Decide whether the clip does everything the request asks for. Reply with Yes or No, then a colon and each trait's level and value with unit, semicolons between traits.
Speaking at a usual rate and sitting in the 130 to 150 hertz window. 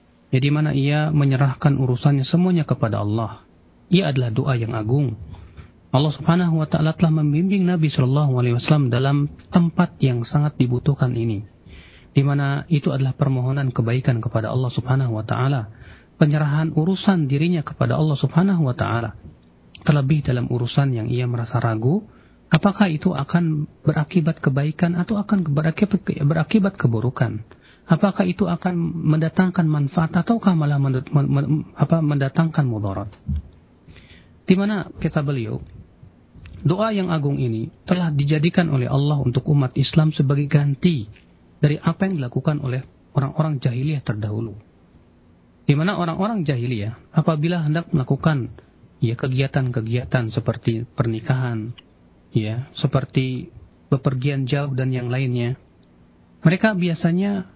Yes: average, 125 wpm; medium, 140 Hz